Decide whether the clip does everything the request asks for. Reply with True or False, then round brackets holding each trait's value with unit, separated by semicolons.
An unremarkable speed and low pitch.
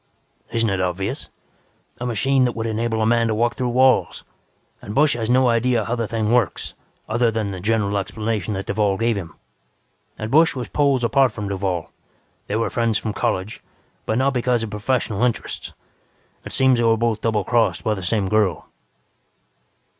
True (180 wpm; 115 Hz)